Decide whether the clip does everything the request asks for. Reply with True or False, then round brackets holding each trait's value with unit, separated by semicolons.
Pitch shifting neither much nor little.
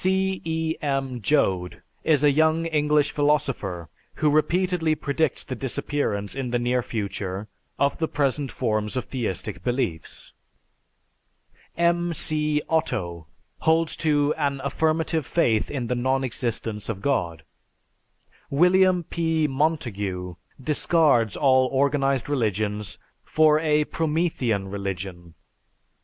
False (6.2 semitones)